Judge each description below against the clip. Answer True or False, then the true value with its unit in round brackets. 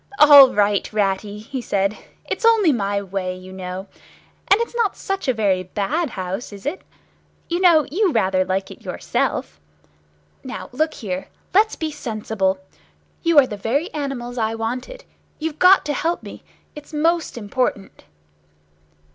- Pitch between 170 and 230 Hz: False (240 Hz)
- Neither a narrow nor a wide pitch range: False (8.2 semitones)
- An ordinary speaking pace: True (155 wpm)